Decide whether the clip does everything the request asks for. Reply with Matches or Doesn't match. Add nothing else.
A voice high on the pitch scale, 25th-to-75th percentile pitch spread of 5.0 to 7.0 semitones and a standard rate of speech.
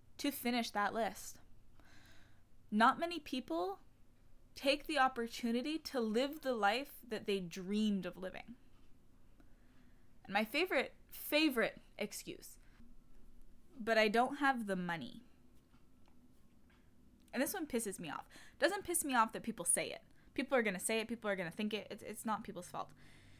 Matches